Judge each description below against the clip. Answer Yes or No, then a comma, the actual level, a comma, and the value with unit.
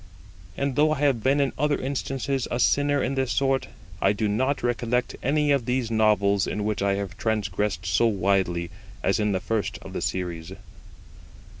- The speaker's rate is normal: Yes, average, 180 wpm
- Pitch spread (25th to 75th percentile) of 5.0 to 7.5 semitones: Yes, average, 5.3 semitones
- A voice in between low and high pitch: No, low, 115 Hz